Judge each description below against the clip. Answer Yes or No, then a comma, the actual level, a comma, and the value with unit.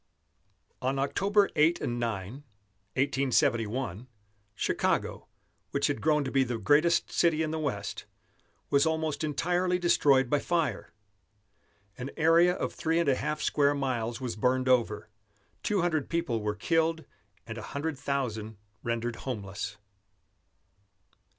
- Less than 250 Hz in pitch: Yes, low, 135 Hz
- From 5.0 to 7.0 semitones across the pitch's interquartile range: Yes, wide, 5.5 semitones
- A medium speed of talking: No, slow, 130 wpm